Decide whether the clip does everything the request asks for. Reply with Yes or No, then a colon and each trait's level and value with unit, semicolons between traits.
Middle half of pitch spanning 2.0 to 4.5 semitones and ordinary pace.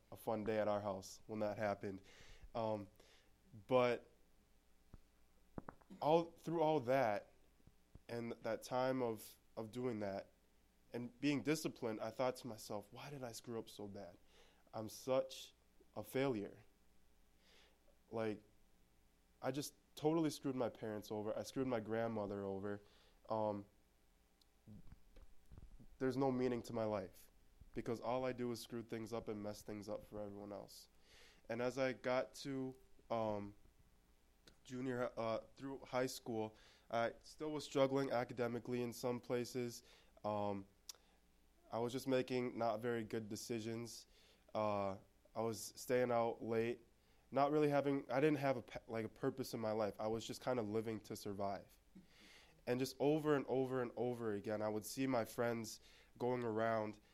Yes: average, 3.7 semitones; average, 150 wpm